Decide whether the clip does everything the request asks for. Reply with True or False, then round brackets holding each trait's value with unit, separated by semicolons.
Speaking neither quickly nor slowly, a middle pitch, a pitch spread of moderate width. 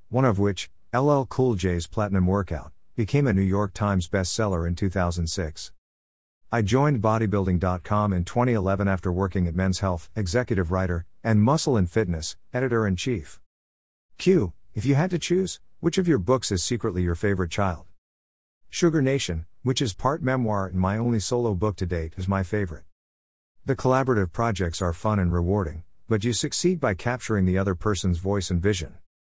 False (170 wpm; 100 Hz; 5.0 semitones)